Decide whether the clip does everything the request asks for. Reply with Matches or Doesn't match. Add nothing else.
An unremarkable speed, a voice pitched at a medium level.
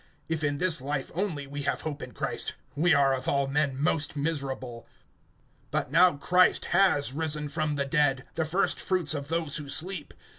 Matches